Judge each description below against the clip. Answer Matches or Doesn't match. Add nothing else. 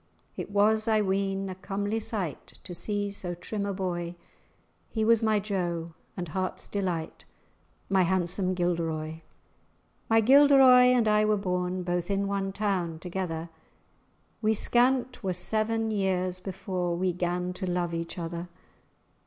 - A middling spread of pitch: Matches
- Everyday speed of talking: Matches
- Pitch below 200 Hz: Matches